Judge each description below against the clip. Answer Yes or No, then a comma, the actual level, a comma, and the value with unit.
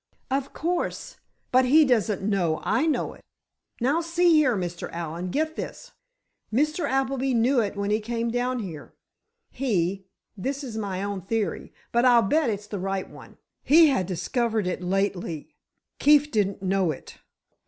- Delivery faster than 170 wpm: No, average, 155 wpm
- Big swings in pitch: Yes, wide, 5.9 semitones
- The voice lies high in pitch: Yes, high, 225 Hz